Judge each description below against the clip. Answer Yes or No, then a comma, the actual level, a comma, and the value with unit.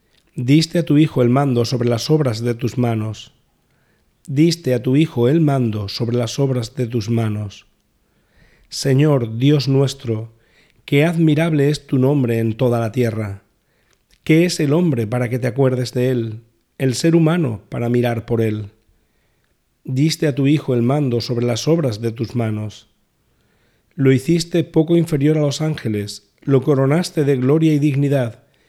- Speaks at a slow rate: No, average, 165 wpm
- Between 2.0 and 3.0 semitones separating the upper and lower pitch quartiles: No, average, 4.3 semitones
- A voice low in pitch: Yes, low, 130 Hz